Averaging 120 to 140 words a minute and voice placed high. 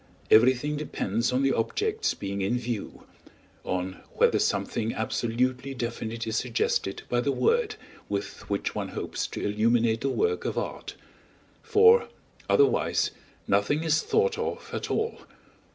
No: slow, 135 wpm; low, 125 Hz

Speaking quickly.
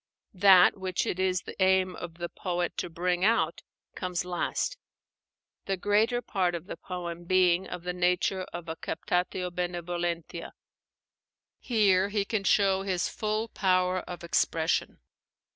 No: average, 145 wpm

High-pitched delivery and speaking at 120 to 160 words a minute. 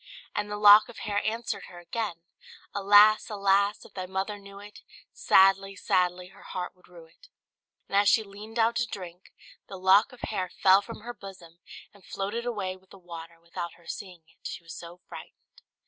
No: high, 195 Hz; average, 195 wpm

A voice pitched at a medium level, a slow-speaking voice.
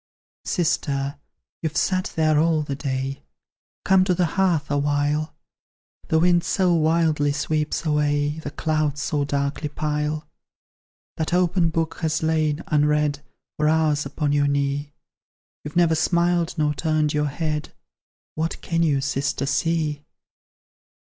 Yes: medium, 155 Hz; slow, 130 wpm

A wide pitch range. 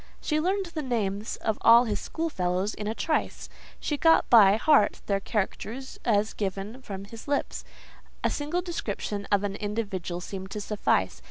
Yes: wide, 5.7 semitones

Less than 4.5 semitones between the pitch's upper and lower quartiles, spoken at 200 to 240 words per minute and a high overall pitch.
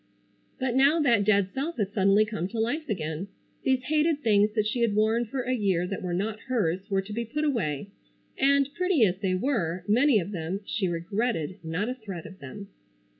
No: average, 5.1 semitones; fast, 205 wpm; high, 215 Hz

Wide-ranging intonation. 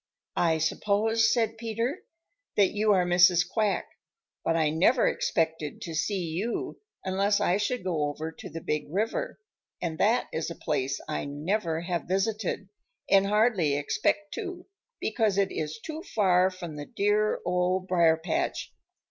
No: average, 4.7 semitones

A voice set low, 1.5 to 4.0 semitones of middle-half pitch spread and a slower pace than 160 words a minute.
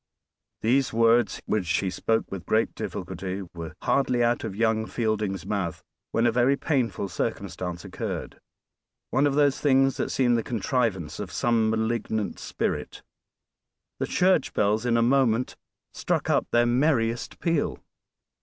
Yes: low, 115 Hz; average, 3.5 semitones; average, 145 wpm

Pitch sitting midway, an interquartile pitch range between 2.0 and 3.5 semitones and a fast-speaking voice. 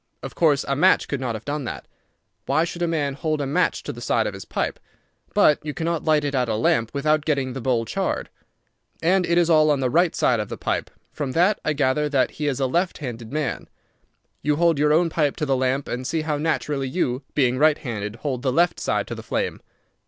Yes: medium, 145 Hz; average, 3.2 semitones; fast, 240 wpm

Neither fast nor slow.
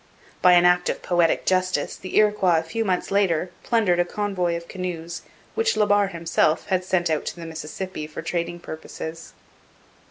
Yes: average, 180 wpm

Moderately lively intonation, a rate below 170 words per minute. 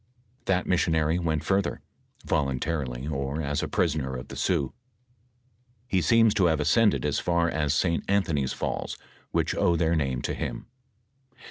Yes: average, 3.9 semitones; average, 150 wpm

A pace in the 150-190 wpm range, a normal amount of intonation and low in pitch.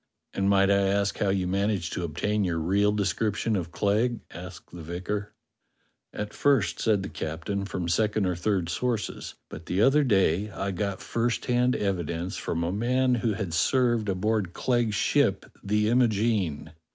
Yes: average, 170 wpm; average, 3.3 semitones; low, 100 Hz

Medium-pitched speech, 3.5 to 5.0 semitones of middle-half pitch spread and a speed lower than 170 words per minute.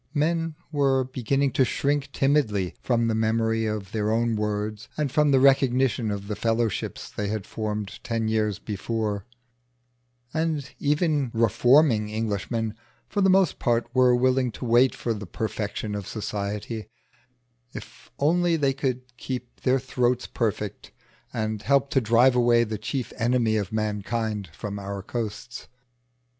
No: low, 115 Hz; average, 3.8 semitones; average, 145 wpm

